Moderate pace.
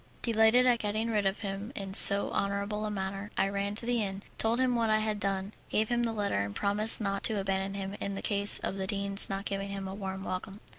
No: fast, 245 wpm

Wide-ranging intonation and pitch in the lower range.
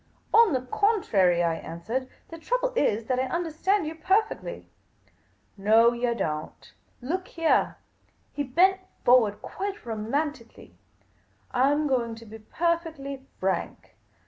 No: wide, 7.3 semitones; very high, 260 Hz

